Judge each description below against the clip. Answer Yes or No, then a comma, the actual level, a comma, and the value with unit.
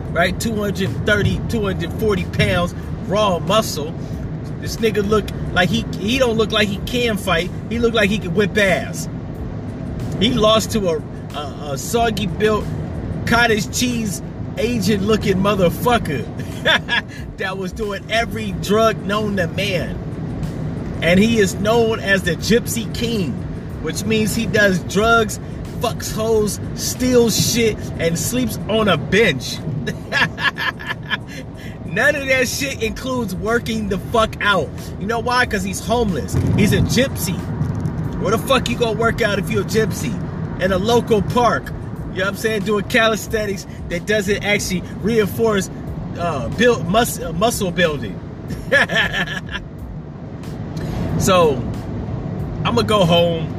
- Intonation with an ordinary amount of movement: Yes, average, 3.4 semitones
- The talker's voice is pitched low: No, high, 210 Hz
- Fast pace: No, slow, 135 wpm